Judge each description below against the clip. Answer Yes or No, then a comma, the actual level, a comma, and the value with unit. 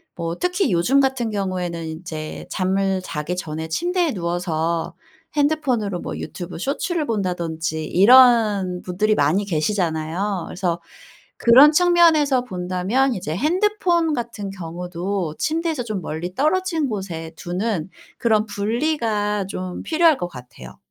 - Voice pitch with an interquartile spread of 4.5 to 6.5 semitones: No, wide, 7.4 semitones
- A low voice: No, high, 195 Hz